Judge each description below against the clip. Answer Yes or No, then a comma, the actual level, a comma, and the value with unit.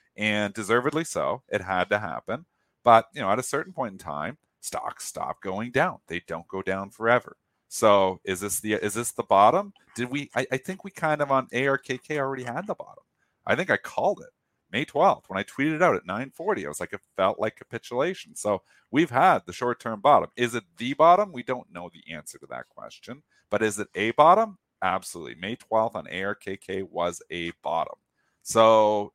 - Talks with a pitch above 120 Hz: No, low, 115 Hz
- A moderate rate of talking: No, fast, 210 wpm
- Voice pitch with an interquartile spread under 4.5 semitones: No, average, 4.9 semitones